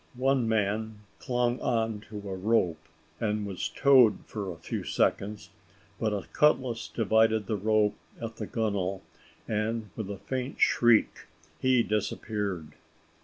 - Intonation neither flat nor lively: No, narrow, 2.2 semitones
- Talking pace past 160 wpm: No, slow, 135 wpm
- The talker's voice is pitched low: Yes, low, 110 Hz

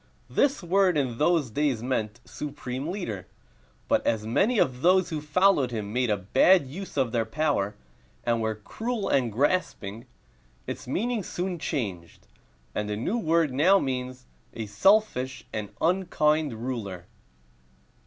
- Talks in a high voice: No, low, 130 Hz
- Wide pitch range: Yes, wide, 7.7 semitones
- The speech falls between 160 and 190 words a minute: No, average, 140 wpm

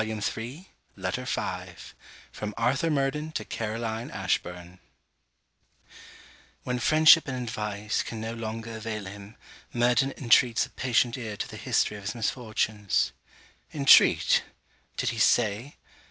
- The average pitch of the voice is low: Yes, low, 115 Hz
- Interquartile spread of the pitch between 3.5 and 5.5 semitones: No, average, 3.0 semitones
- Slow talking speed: Yes, slow, 125 wpm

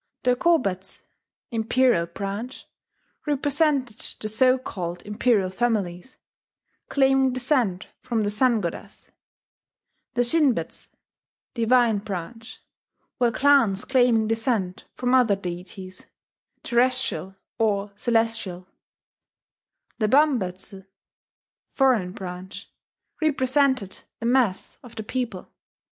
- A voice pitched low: No, high, 225 Hz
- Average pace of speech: No, slow, 95 wpm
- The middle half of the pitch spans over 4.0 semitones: Yes, average, 4.8 semitones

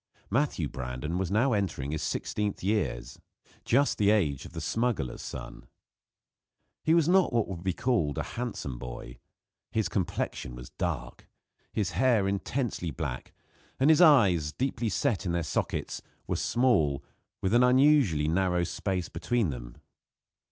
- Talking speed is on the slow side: No, average, 145 wpm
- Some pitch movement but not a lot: No, wide, 7.6 semitones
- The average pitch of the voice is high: No, very low, 95 Hz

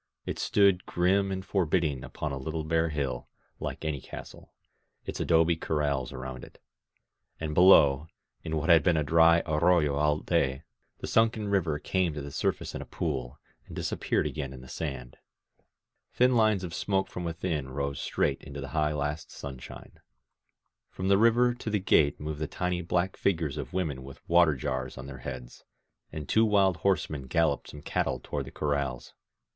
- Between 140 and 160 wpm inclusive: No, average, 180 wpm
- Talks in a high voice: No, very low, 80 Hz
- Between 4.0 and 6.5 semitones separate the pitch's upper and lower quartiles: Yes, average, 4.3 semitones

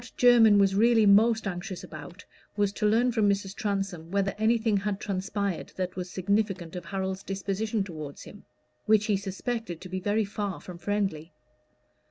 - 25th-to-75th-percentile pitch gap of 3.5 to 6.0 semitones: No, narrow, 2.4 semitones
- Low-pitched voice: No, high, 200 Hz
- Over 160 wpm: Yes, average, 170 wpm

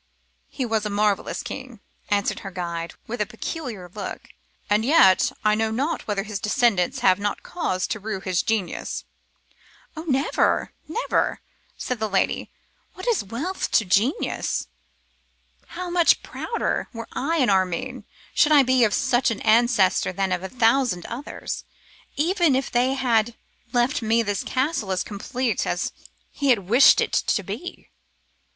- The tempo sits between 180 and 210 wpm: No, average, 155 wpm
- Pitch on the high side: Yes, high, 230 Hz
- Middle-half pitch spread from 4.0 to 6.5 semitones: Yes, average, 4.7 semitones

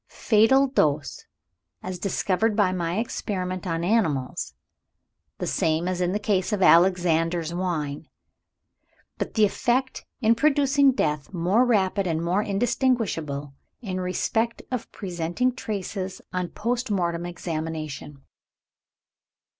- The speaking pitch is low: No, medium, 185 Hz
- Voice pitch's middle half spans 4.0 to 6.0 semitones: Yes, average, 4.8 semitones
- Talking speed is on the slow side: Yes, slow, 115 wpm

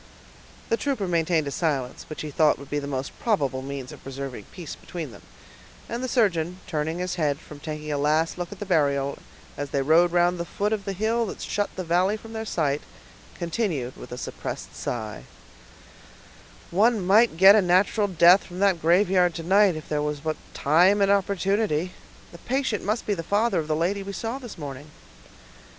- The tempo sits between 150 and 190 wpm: No, average, 200 wpm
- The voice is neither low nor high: Yes, medium, 175 Hz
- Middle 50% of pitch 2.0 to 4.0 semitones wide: No, average, 5.1 semitones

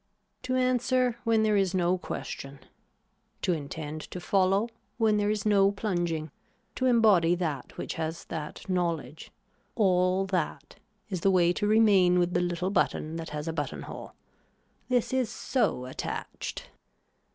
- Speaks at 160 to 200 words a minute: No, average, 150 wpm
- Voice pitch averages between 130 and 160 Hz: No, medium, 185 Hz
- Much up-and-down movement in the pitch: No, average, 4.2 semitones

